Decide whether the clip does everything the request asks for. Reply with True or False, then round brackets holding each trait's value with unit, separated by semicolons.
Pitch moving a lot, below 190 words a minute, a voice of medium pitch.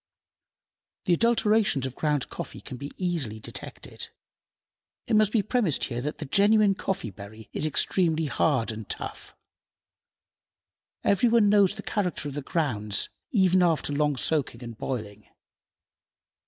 True (8.1 semitones; 140 wpm; 155 Hz)